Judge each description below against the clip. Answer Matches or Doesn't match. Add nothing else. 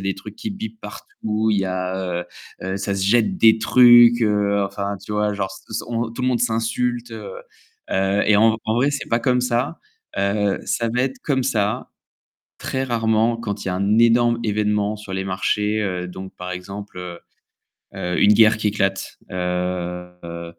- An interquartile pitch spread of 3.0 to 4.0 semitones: Matches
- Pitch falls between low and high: Doesn't match